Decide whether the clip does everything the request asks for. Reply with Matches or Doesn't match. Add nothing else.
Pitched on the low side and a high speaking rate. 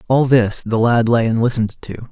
Matches